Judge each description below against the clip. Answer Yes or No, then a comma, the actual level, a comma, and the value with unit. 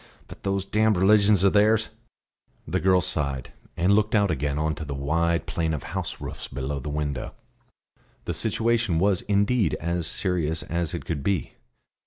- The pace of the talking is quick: No, average, 175 wpm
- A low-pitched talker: Yes, very low, 85 Hz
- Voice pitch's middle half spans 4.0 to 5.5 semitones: Yes, average, 4.7 semitones